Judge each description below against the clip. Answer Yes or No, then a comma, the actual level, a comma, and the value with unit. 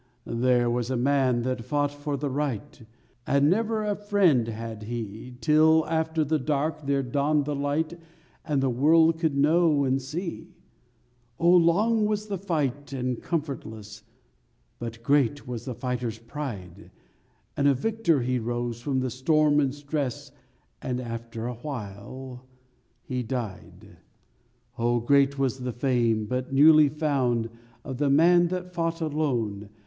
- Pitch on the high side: No, medium, 140 Hz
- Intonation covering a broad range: No, average, 4.3 semitones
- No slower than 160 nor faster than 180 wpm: No, average, 145 wpm